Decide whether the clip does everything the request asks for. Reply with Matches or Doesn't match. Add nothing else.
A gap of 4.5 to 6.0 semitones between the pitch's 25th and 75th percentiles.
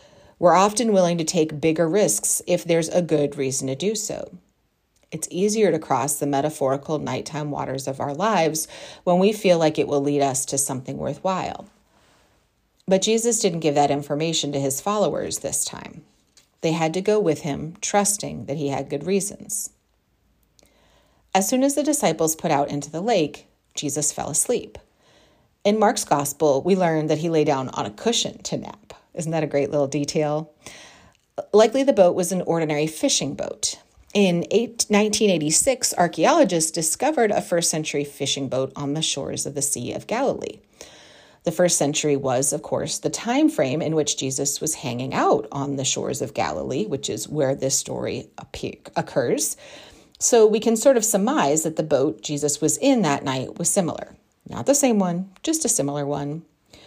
Matches